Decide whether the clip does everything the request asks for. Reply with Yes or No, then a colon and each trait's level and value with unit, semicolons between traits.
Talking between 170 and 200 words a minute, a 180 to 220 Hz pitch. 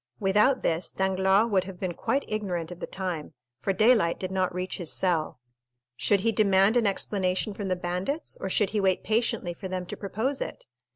Yes: average, 195 wpm; high, 190 Hz